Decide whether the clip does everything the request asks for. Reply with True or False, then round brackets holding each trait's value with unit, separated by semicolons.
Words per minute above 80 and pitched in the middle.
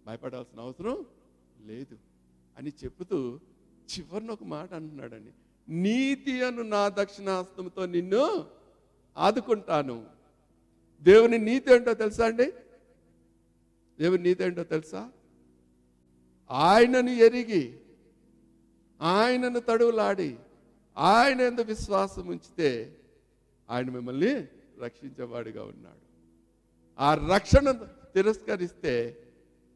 False (75 wpm; 150 Hz)